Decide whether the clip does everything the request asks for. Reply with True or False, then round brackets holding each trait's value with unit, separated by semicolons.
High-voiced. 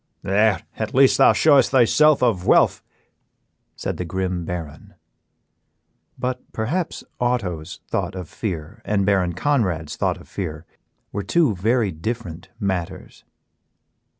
False (100 Hz)